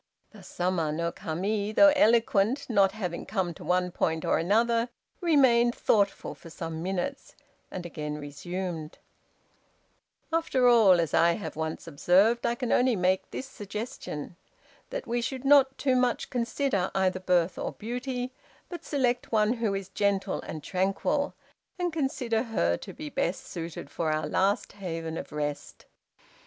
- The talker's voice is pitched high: Yes, high, 200 Hz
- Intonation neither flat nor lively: No, wide, 6.1 semitones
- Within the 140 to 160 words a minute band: Yes, average, 150 wpm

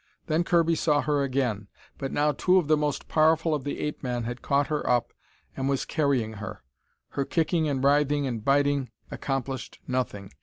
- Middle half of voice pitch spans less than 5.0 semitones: Yes, average, 2.7 semitones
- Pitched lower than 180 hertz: Yes, medium, 140 Hz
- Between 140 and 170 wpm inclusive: No, average, 185 wpm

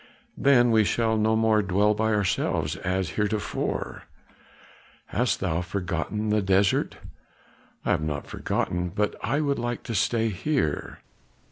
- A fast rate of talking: No, slow, 135 wpm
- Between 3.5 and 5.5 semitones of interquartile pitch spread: No, average, 3.1 semitones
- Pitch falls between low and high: No, low, 105 Hz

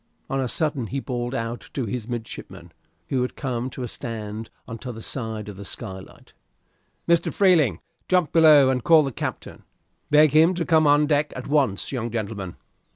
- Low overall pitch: Yes, low, 125 Hz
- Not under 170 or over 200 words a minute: Yes, average, 180 wpm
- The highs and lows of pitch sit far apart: No, average, 4.8 semitones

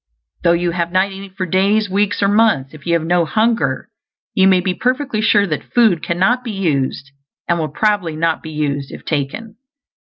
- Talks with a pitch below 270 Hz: Yes, medium, 185 Hz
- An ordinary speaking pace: Yes, average, 195 wpm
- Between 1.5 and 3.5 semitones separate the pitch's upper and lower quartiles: No, average, 4.4 semitones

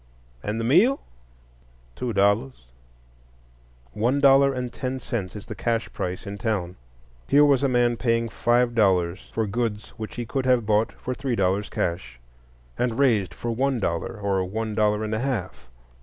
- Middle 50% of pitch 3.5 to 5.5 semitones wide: Yes, average, 3.8 semitones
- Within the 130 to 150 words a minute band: No, average, 170 wpm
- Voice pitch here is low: Yes, low, 115 Hz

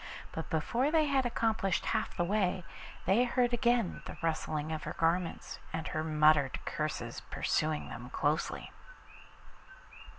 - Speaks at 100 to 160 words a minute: Yes, slow, 135 wpm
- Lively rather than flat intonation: Yes, wide, 7.1 semitones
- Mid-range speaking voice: Yes, medium, 170 Hz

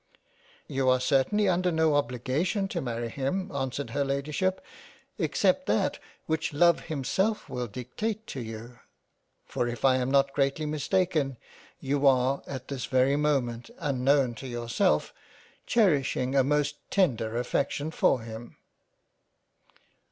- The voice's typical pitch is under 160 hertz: Yes, medium, 140 Hz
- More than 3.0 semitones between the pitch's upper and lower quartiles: Yes, average, 3.7 semitones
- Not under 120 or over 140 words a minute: Yes, slow, 135 wpm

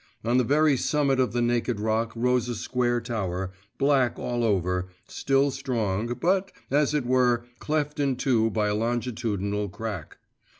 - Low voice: Yes, low, 120 Hz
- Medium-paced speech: Yes, average, 160 wpm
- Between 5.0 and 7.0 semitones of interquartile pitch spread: No, average, 3.6 semitones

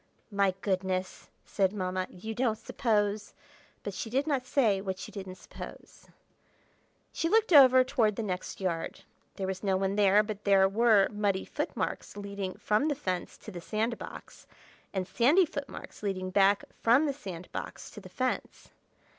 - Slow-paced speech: No, average, 165 wpm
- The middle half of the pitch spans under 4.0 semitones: Yes, average, 3.5 semitones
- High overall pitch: Yes, high, 205 Hz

